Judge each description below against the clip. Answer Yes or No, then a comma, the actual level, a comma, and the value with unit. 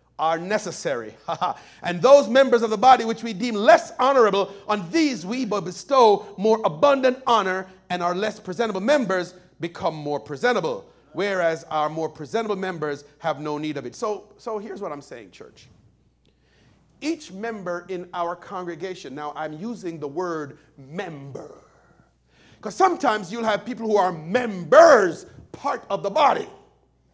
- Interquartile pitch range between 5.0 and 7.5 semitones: Yes, wide, 5.4 semitones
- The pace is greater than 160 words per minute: No, average, 155 wpm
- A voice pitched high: Yes, high, 195 Hz